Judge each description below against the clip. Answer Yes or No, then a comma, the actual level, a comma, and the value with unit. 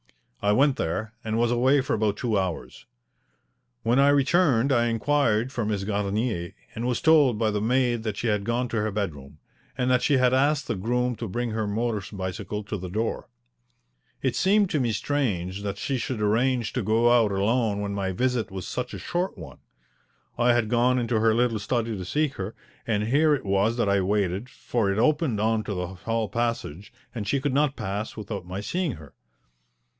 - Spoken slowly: No, average, 200 wpm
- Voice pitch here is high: No, low, 115 Hz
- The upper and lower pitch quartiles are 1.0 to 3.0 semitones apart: No, average, 3.6 semitones